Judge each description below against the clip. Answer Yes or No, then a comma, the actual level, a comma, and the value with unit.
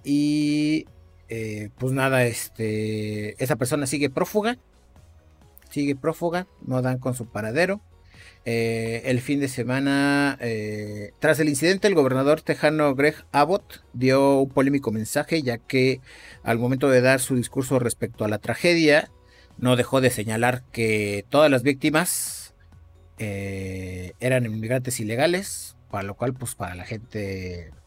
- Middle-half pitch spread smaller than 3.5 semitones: No, average, 5.0 semitones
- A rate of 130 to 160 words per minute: Yes, average, 140 wpm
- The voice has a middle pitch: No, low, 125 Hz